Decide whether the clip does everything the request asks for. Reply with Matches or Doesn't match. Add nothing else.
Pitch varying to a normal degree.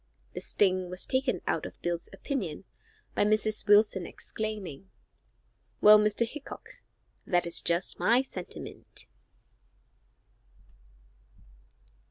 Matches